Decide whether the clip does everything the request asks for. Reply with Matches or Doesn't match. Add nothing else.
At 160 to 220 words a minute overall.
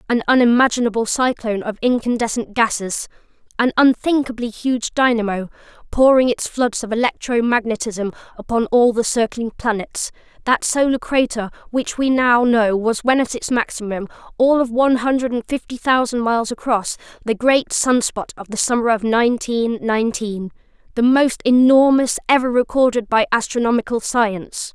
Doesn't match